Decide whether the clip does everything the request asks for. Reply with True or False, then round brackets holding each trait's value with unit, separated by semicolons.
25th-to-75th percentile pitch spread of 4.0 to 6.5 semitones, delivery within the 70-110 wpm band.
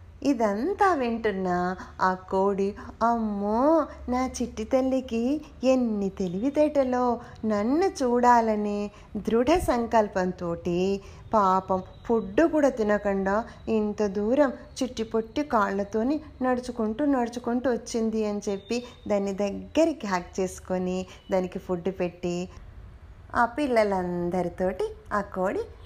True (4.8 semitones; 90 wpm)